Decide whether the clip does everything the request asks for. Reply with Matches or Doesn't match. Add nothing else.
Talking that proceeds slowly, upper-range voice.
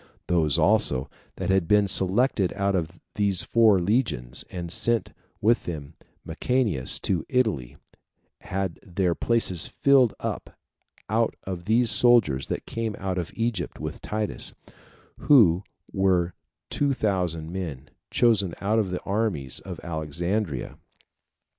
Doesn't match